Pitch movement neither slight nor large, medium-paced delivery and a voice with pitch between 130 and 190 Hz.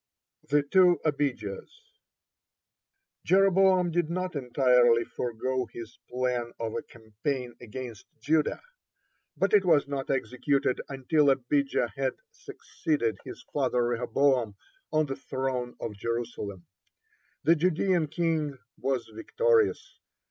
No: average, 4.8 semitones; slow, 110 wpm; low, 135 Hz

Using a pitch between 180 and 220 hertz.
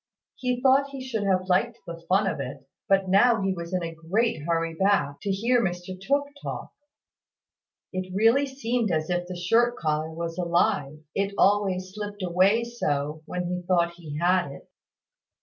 Yes: medium, 185 Hz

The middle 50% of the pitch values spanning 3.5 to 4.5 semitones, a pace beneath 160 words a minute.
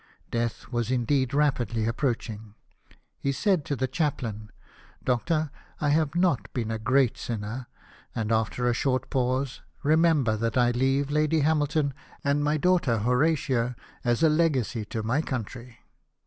Yes: average, 4.1 semitones; average, 150 wpm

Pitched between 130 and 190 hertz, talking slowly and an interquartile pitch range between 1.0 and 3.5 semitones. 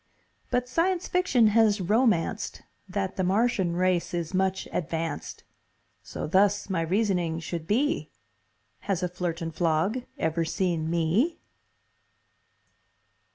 No: medium, 185 Hz; slow, 110 wpm; average, 4.4 semitones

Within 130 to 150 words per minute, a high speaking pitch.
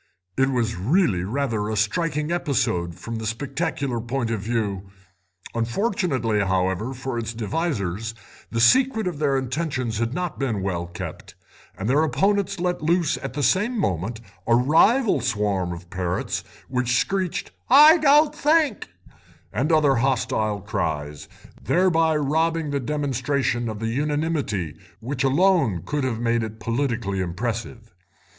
No: average, 140 wpm; low, 125 Hz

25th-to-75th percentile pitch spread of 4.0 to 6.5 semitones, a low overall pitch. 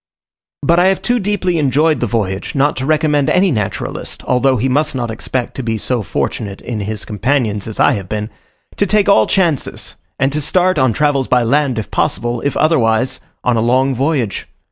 Yes: average, 5.1 semitones; low, 130 Hz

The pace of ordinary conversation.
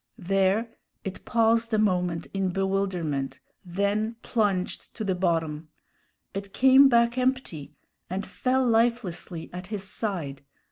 No: slow, 125 wpm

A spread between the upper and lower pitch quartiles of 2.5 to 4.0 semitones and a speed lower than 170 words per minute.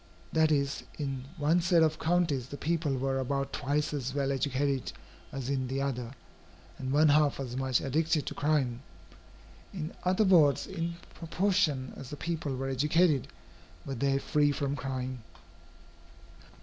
Yes: average, 2.9 semitones; average, 150 wpm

